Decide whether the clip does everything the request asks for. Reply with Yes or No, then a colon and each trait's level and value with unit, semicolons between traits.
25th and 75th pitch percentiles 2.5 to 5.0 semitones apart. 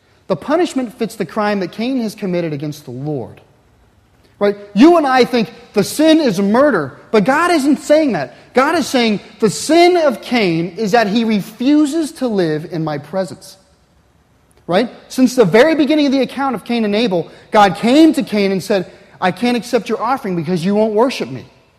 No: wide, 5.6 semitones